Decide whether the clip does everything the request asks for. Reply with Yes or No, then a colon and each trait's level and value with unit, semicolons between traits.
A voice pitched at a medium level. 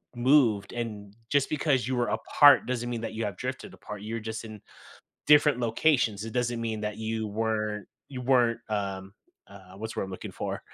No: low, 115 Hz